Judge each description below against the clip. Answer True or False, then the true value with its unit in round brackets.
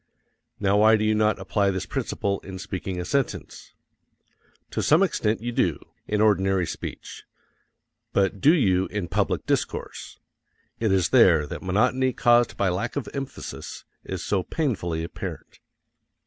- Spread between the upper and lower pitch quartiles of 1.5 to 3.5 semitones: False (4.1 semitones)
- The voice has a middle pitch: False (100 Hz)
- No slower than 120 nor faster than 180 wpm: True (150 wpm)